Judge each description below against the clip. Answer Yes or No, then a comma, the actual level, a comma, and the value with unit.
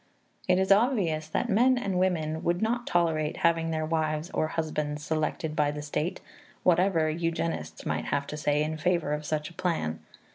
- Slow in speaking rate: No, average, 180 wpm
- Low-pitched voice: No, medium, 160 Hz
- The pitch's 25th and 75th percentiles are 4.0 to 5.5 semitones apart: No, average, 2.9 semitones